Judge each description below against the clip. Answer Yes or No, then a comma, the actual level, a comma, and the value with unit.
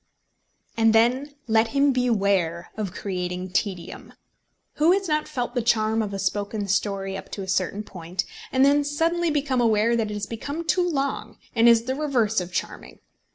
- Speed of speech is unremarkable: Yes, average, 180 wpm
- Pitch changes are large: Yes, wide, 5.7 semitones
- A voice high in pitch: Yes, high, 225 Hz